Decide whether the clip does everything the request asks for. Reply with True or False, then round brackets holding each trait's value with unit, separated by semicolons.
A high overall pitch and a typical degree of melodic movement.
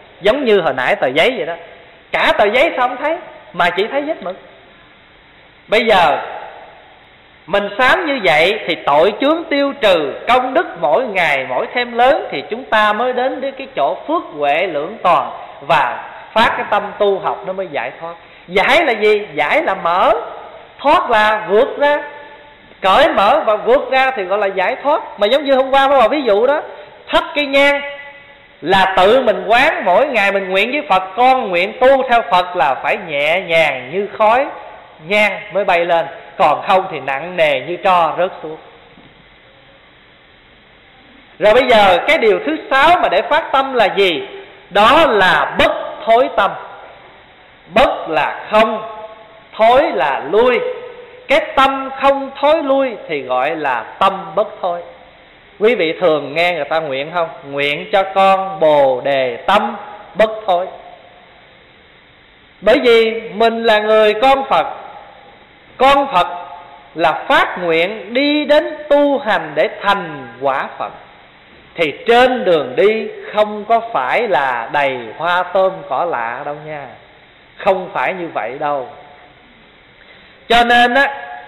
False (220 Hz; 6.7 semitones)